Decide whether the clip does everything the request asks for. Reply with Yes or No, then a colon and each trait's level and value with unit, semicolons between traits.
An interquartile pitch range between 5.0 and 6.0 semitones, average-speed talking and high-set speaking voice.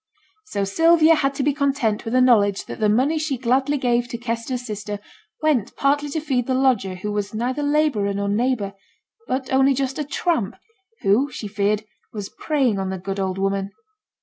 Yes: average, 5.3 semitones; average, 190 wpm; high, 245 Hz